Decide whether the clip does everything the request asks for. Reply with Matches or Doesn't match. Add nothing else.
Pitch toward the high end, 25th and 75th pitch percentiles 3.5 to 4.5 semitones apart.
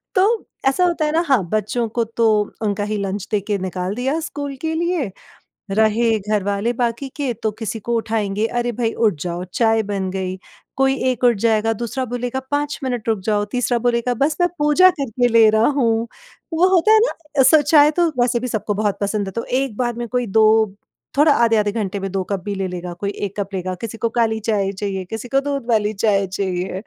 Matches